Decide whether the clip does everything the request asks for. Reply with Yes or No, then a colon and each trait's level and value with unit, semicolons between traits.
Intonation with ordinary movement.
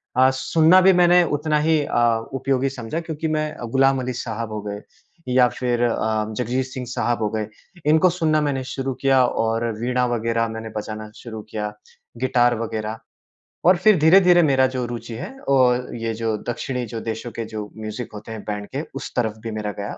Yes: average, 3.4 semitones